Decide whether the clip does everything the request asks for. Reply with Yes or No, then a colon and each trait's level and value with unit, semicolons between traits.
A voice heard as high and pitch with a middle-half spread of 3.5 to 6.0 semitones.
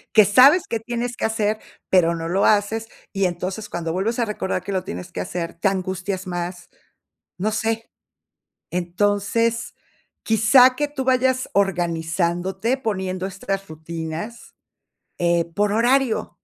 Yes: high, 195 Hz; average, 4.3 semitones